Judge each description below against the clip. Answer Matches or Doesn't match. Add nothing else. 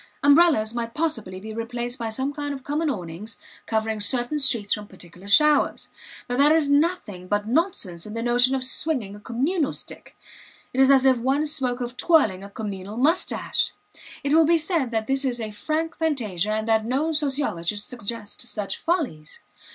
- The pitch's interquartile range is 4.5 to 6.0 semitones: Matches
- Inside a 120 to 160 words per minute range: Doesn't match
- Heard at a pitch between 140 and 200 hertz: Doesn't match